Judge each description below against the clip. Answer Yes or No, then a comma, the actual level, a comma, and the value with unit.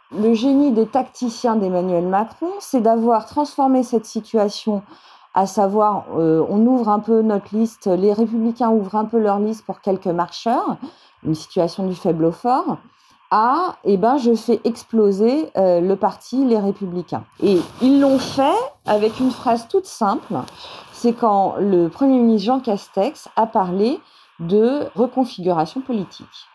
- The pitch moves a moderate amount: Yes, average, 4.6 semitones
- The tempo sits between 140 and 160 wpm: Yes, average, 155 wpm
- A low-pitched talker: No, high, 220 Hz